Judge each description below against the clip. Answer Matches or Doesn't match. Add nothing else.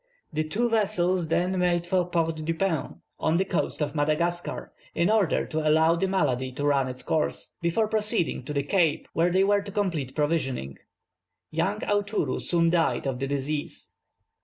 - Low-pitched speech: Doesn't match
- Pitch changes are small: Doesn't match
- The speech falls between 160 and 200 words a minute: Matches